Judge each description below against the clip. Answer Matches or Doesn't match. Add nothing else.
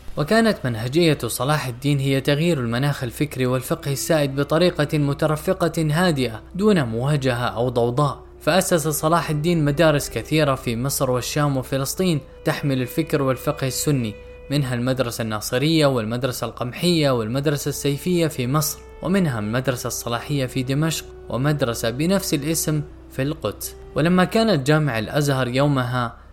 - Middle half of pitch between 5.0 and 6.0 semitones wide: Doesn't match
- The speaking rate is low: Doesn't match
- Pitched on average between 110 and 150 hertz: Matches